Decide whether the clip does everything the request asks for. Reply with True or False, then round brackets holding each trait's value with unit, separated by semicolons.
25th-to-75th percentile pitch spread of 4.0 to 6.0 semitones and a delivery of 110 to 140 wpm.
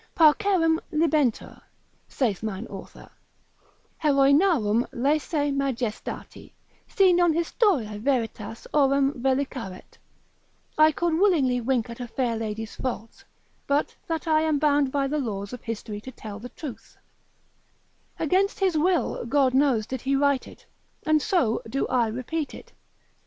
True (5.0 semitones; 135 wpm)